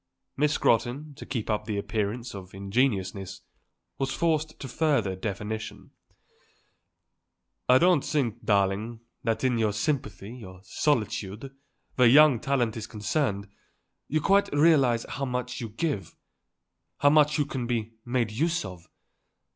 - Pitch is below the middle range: Yes, low, 120 Hz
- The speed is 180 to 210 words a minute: No, slow, 135 wpm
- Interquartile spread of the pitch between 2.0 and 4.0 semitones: No, average, 5.3 semitones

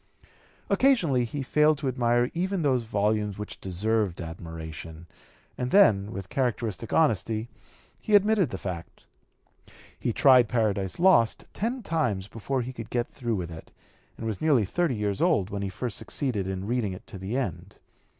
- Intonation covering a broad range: Yes, wide, 5.8 semitones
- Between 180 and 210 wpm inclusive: No, average, 160 wpm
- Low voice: Yes, low, 115 Hz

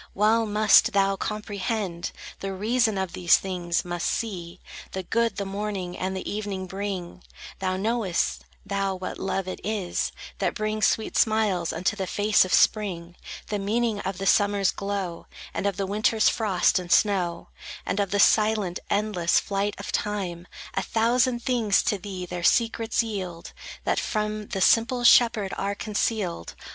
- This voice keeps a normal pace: Yes, average, 160 wpm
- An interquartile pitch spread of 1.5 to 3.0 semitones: Yes, narrow, 2.4 semitones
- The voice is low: No, high, 200 Hz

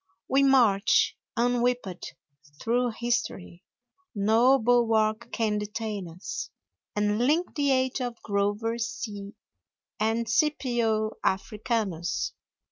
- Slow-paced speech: Yes, slow, 95 wpm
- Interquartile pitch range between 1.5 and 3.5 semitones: Yes, average, 2.8 semitones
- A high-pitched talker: Yes, high, 225 Hz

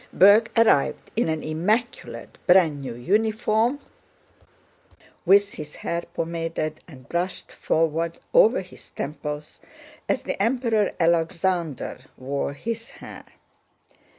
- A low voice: No, medium, 170 Hz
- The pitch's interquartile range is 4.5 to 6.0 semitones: Yes, wide, 5.6 semitones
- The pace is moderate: No, slow, 105 wpm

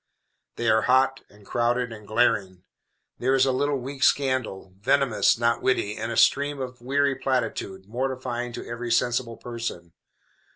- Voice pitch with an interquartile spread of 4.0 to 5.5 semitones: No, average, 2.7 semitones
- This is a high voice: No, low, 120 Hz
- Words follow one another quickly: No, average, 155 wpm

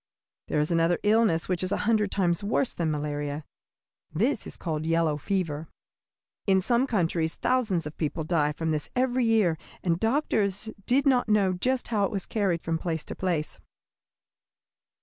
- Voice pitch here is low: No, medium, 180 Hz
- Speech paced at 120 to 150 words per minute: No, average, 170 wpm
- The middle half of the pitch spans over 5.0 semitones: Yes, wide, 5.4 semitones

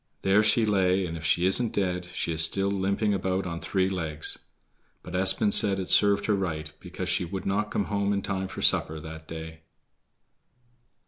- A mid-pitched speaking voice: No, very low, 95 Hz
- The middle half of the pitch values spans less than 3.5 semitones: Yes, average, 2.7 semitones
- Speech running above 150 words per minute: Yes, average, 190 wpm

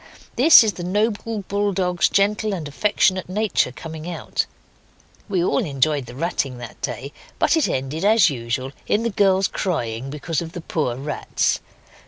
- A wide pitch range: Yes, wide, 6.6 semitones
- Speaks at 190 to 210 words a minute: No, average, 165 wpm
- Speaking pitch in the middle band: Yes, medium, 175 Hz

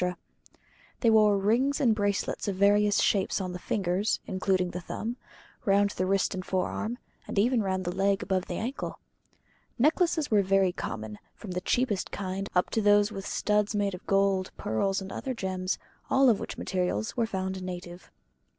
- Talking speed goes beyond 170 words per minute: Yes, average, 180 wpm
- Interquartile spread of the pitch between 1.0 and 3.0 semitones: Yes, narrow, 2.4 semitones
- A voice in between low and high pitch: No, high, 195 Hz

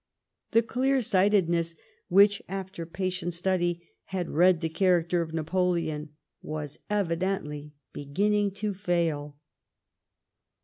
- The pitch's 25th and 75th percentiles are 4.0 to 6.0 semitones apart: No, average, 3.1 semitones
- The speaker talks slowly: Yes, slow, 100 wpm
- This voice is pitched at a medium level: Yes, medium, 175 Hz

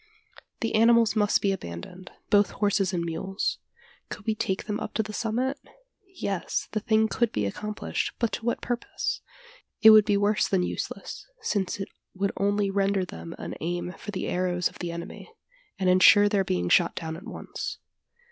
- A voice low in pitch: No, high, 200 Hz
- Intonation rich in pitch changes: No, average, 3.1 semitones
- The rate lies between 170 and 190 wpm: Yes, average, 180 wpm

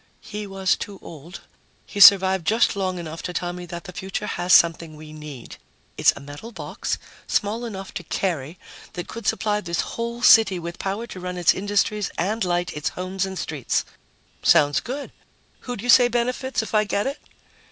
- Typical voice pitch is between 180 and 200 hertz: Yes, high, 190 Hz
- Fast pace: No, average, 185 wpm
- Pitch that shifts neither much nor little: Yes, average, 3.8 semitones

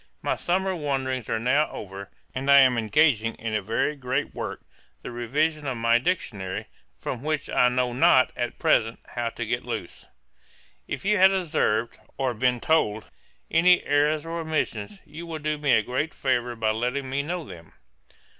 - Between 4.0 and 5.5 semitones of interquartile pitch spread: Yes, average, 4.7 semitones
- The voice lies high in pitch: No, low, 130 Hz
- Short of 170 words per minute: No, average, 175 wpm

